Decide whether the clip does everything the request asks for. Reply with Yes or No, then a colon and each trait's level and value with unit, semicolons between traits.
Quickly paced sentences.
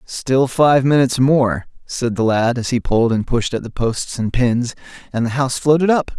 Yes: fast, 215 wpm